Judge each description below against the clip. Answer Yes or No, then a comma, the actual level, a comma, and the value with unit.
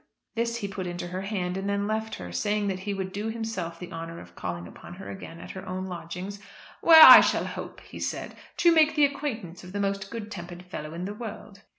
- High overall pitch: Yes, high, 195 Hz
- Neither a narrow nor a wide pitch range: Yes, average, 3.4 semitones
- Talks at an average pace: No, fast, 235 wpm